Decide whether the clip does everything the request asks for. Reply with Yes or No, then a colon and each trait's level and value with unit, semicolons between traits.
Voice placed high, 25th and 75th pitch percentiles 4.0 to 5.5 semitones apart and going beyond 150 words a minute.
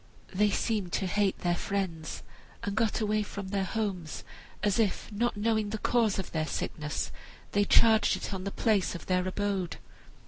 No: high, 200 Hz; narrow, 2.5 semitones; average, 175 wpm